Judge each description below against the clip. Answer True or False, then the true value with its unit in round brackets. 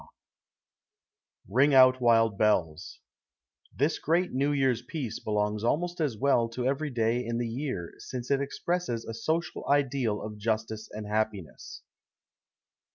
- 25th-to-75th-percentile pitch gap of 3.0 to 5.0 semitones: True (4.4 semitones)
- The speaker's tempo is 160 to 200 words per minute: False (140 wpm)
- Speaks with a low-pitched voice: True (120 Hz)